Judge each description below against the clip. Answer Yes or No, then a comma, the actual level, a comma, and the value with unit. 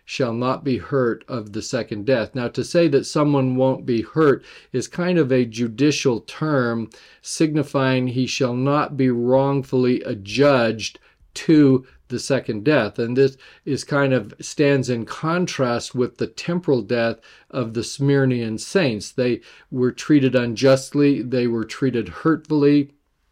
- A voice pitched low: Yes, low, 130 Hz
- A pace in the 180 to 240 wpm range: No, average, 145 wpm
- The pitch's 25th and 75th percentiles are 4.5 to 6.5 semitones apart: No, average, 3.0 semitones